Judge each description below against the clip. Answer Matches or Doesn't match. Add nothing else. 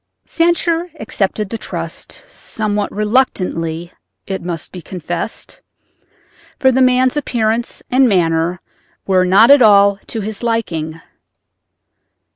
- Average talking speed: Doesn't match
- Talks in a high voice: Matches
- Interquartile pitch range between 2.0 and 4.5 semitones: Doesn't match